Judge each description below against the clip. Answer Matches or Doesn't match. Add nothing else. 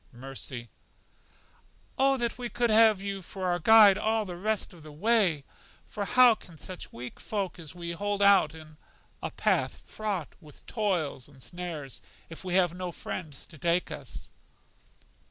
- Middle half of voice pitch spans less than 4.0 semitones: Doesn't match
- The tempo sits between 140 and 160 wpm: Doesn't match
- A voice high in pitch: Doesn't match